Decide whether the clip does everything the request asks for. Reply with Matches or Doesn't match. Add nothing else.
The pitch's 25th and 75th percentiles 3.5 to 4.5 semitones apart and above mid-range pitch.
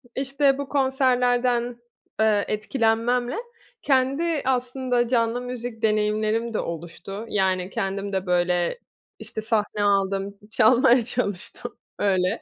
Matches